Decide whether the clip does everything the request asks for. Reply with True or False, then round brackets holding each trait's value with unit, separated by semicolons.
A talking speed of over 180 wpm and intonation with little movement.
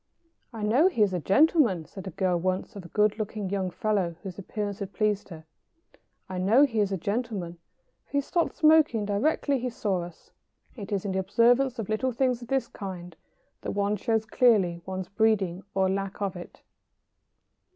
False (190 wpm; 3.7 semitones)